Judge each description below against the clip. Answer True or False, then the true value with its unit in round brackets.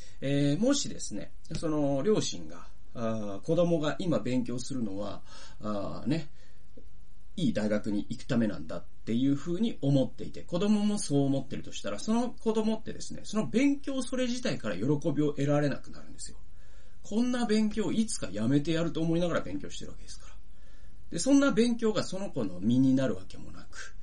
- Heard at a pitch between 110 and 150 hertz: True (140 Hz)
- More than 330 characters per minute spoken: True (365 characters per minute)